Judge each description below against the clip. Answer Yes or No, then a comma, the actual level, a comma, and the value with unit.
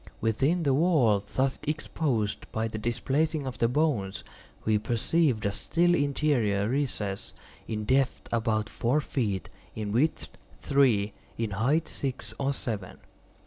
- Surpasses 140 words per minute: No, slow, 135 wpm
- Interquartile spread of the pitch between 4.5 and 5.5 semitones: Yes, average, 5.1 semitones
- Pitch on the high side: No, low, 125 Hz